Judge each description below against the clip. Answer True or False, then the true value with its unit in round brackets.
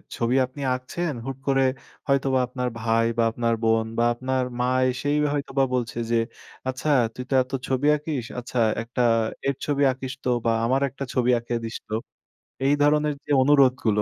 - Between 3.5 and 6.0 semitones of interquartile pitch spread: False (2.5 semitones)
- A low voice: True (130 Hz)